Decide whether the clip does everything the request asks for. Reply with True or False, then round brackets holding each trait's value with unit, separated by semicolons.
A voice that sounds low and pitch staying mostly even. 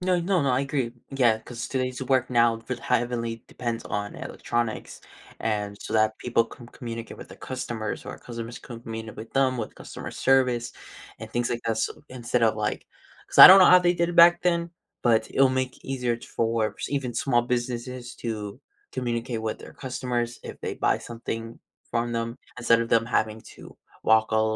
True (120 Hz; 2.2 semitones)